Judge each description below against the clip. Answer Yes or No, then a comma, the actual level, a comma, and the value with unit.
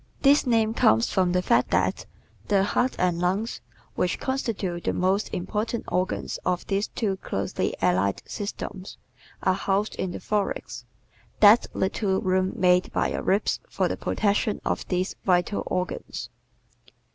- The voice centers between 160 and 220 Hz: Yes, high, 190 Hz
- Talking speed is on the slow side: No, average, 150 wpm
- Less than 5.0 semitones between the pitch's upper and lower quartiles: Yes, narrow, 2.6 semitones